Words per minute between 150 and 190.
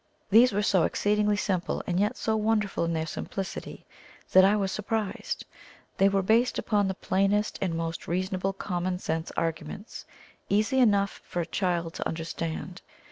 Yes: average, 160 wpm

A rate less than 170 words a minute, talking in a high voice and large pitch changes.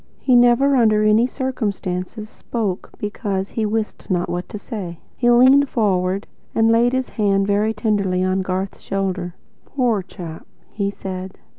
No: average, 150 wpm; high, 210 Hz; average, 3.6 semitones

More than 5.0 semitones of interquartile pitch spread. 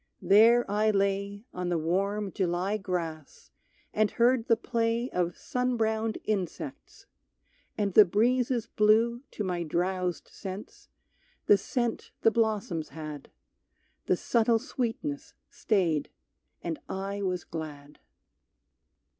No: average, 4.1 semitones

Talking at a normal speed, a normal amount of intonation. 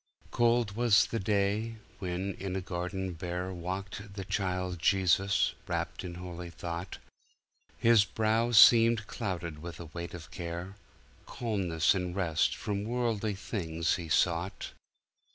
No: slow, 130 wpm; average, 3.1 semitones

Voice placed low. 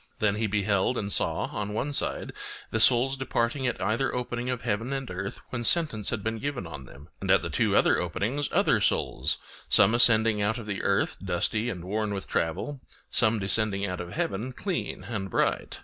Yes: low, 110 Hz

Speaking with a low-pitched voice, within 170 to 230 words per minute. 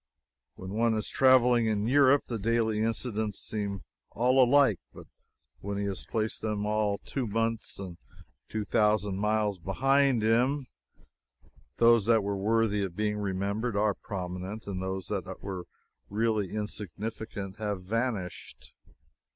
No: low, 105 Hz; slow, 135 wpm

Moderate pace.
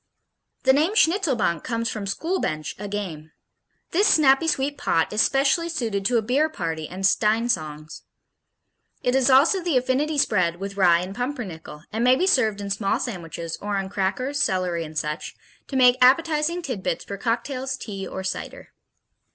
Yes: average, 170 wpm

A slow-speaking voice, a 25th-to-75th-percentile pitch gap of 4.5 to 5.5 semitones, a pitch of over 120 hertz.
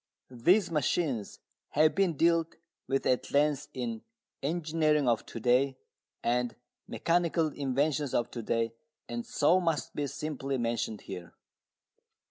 Yes: slow, 125 wpm; average, 5.0 semitones; medium, 140 Hz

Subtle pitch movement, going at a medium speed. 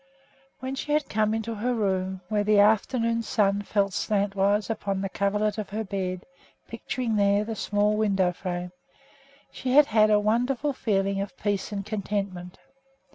Yes: narrow, 2.0 semitones; average, 160 wpm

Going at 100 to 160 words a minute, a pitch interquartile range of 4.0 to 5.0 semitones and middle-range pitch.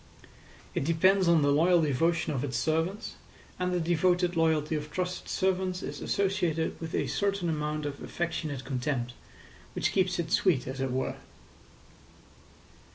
No: average, 150 wpm; average, 3.5 semitones; medium, 165 Hz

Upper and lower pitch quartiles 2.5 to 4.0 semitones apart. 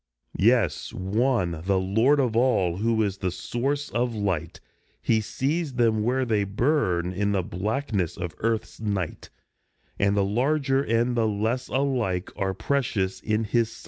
No: average, 4.5 semitones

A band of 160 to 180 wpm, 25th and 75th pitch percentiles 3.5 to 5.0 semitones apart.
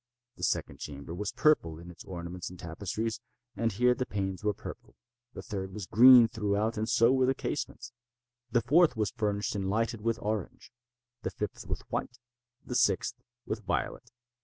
Yes: average, 165 wpm; average, 3.9 semitones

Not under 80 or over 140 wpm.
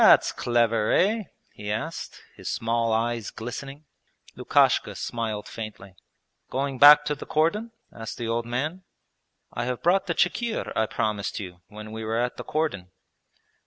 No: average, 155 wpm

